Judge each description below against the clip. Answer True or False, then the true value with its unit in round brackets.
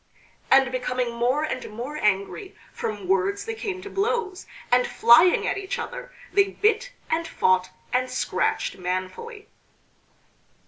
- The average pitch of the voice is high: True (265 Hz)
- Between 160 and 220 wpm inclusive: False (135 wpm)